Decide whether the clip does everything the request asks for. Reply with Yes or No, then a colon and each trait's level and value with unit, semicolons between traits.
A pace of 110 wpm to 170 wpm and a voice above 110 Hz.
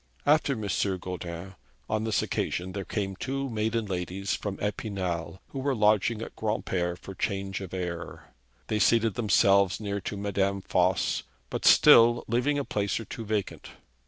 No: average, 160 wpm; low, 100 Hz